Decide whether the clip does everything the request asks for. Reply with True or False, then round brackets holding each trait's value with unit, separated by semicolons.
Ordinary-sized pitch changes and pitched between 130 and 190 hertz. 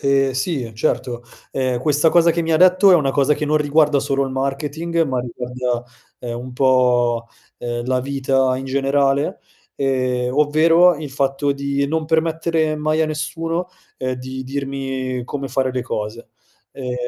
True (3.2 semitones; 135 Hz)